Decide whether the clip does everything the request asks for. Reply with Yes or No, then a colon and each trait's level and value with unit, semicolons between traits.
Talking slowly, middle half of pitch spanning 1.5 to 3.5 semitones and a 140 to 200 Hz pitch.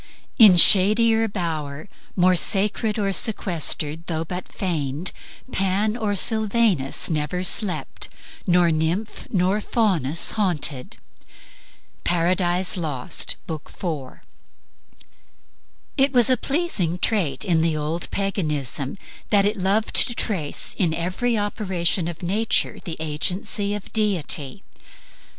No: slow, 110 wpm; average, 4.5 semitones; medium, 185 Hz